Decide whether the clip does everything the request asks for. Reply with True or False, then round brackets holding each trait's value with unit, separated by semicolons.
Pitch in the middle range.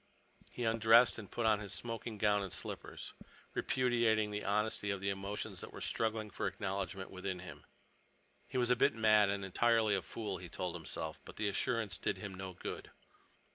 False (105 Hz)